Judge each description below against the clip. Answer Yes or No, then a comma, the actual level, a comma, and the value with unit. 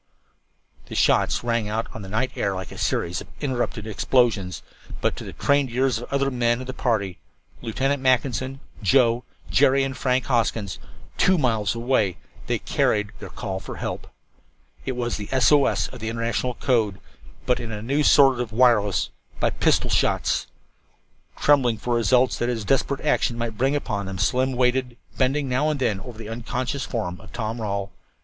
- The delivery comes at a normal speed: Yes, average, 185 wpm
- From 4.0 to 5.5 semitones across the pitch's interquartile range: No, average, 3.2 semitones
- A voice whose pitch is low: Yes, low, 120 Hz